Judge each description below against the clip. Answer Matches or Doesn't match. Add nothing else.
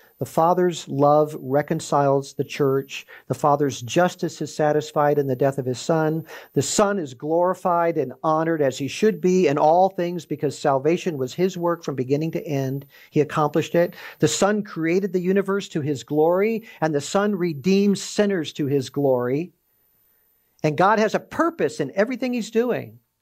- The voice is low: Doesn't match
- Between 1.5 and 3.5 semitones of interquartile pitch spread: Doesn't match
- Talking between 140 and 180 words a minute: Matches